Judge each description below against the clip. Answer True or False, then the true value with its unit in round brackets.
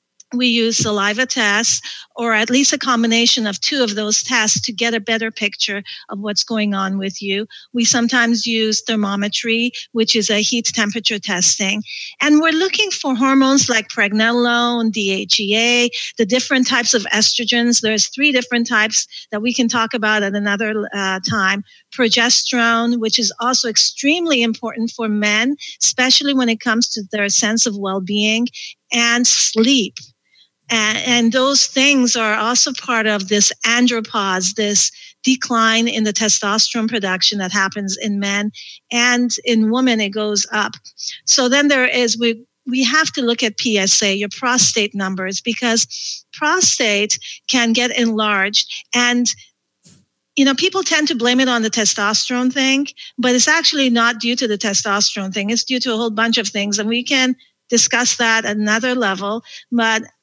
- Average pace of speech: True (160 wpm)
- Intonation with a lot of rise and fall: False (2.7 semitones)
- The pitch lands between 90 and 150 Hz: False (230 Hz)